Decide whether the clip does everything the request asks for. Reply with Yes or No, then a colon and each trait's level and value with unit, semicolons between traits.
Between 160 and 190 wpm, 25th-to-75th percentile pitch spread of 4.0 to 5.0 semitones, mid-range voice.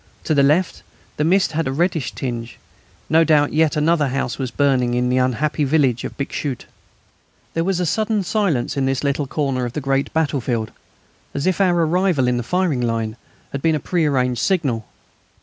Yes: average, 185 wpm; average, 4.4 semitones; medium, 145 Hz